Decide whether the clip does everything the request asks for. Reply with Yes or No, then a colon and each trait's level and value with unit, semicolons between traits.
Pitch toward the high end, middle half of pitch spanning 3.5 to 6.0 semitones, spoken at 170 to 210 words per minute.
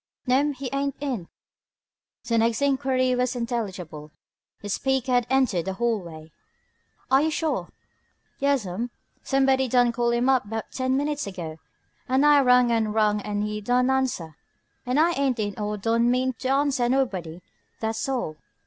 No: high, 245 Hz; average, 4.1 semitones; average, 160 wpm